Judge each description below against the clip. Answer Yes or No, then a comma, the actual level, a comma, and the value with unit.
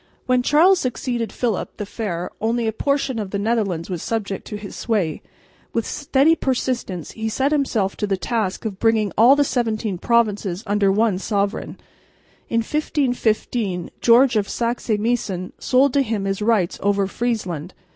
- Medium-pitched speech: No, high, 220 Hz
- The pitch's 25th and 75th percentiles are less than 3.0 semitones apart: No, average, 3.6 semitones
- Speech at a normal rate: Yes, average, 160 wpm